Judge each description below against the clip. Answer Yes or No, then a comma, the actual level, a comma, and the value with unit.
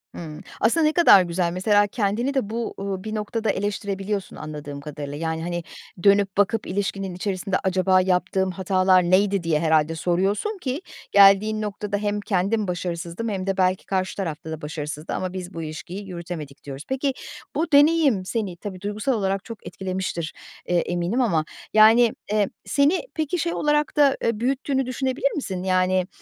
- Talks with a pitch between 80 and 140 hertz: No, high, 195 Hz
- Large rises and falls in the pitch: No, average, 3.6 semitones